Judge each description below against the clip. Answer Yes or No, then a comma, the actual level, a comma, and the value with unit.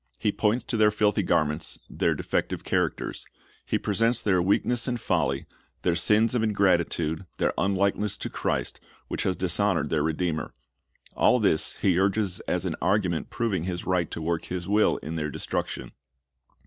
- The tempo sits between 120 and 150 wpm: No, average, 165 wpm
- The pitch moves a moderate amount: Yes, average, 4.0 semitones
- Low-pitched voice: Yes, very low, 95 Hz